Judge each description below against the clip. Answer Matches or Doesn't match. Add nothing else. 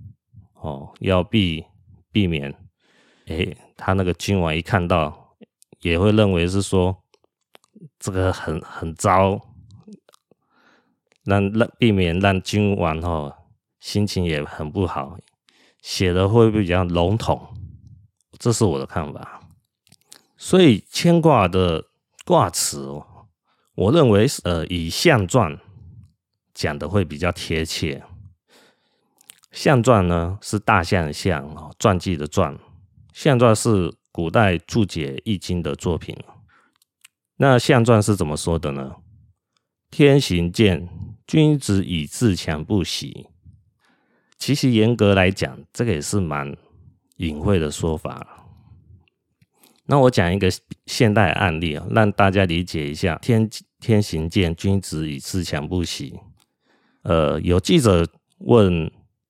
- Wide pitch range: Doesn't match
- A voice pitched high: Doesn't match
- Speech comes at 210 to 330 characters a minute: Doesn't match